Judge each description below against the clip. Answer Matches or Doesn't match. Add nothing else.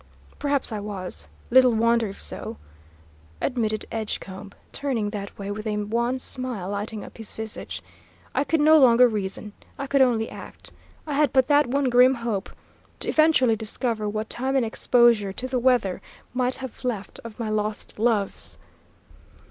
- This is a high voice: Matches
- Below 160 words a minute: Doesn't match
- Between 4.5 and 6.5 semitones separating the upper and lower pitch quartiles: Doesn't match